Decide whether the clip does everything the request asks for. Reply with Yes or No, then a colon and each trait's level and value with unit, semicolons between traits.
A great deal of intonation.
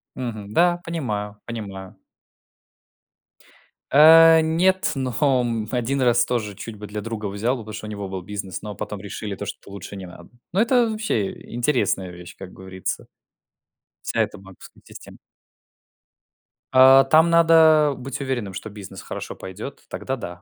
Yes: wide, 5.8 semitones